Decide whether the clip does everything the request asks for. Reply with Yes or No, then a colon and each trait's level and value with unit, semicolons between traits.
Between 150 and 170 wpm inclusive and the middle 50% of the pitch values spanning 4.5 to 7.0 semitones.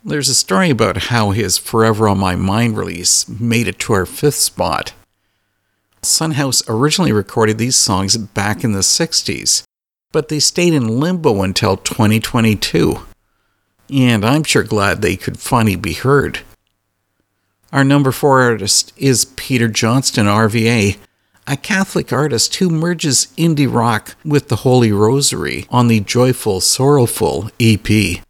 No: average, 140 wpm; average, 4.9 semitones